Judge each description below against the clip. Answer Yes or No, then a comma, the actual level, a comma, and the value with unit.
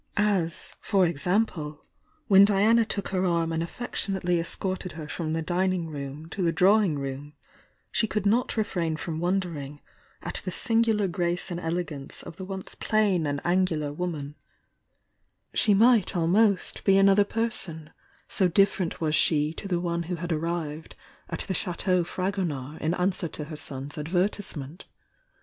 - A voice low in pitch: No, medium, 175 Hz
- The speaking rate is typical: Yes, average, 165 wpm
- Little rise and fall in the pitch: No, average, 3.7 semitones